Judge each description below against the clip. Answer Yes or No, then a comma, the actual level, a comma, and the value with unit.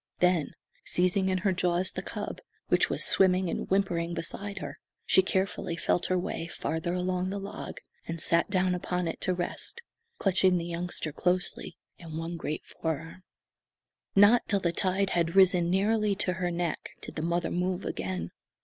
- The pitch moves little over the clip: Yes, narrow, 2.0 semitones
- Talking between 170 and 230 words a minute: Yes, average, 175 wpm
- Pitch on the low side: No, medium, 180 Hz